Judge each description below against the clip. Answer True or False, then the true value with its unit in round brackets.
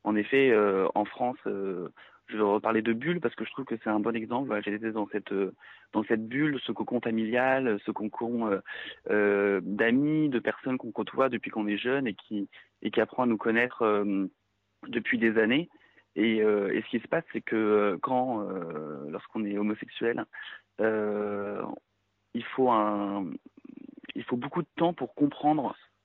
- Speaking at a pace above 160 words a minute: True (190 wpm)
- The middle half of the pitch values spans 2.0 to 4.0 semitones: True (3.5 semitones)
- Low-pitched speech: True (110 Hz)